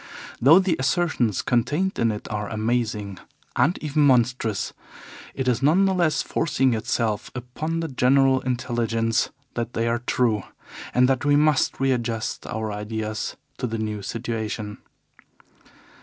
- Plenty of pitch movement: No, average, 3.6 semitones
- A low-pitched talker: Yes, low, 120 Hz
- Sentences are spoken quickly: No, average, 140 wpm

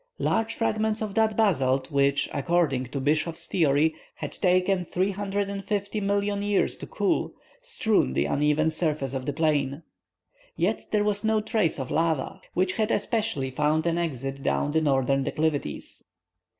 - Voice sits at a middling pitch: Yes, medium, 165 Hz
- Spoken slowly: No, average, 145 wpm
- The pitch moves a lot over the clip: Yes, wide, 6.4 semitones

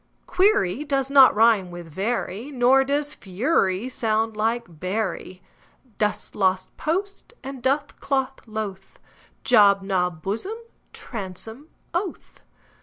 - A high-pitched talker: Yes, high, 225 Hz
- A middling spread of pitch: No, wide, 6.1 semitones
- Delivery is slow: Yes, slow, 110 wpm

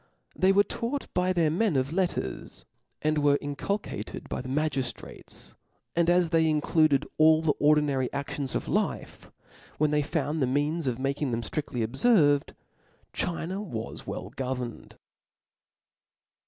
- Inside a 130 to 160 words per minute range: Yes, average, 140 wpm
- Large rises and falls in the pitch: No, average, 3.8 semitones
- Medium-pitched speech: Yes, medium, 150 Hz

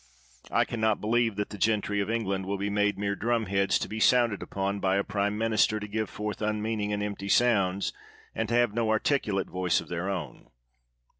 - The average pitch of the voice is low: Yes, low, 105 Hz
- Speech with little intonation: Yes, narrow, 1.9 semitones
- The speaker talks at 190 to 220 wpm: Yes, fast, 205 wpm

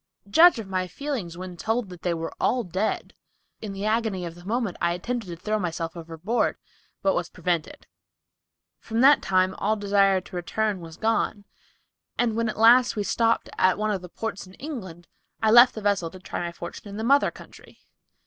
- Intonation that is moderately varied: Yes, average, 4.0 semitones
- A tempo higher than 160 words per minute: Yes, average, 195 wpm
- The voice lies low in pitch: No, high, 200 Hz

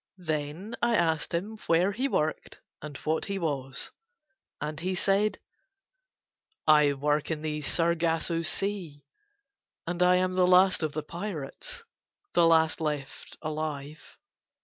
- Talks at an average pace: No, slow, 130 wpm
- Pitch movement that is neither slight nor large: Yes, average, 3.3 semitones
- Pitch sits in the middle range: Yes, medium, 165 Hz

